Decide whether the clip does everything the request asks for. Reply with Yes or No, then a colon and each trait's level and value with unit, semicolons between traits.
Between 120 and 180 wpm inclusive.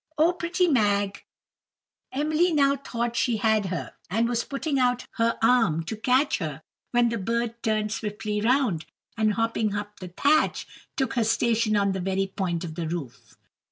Yes: average, 170 wpm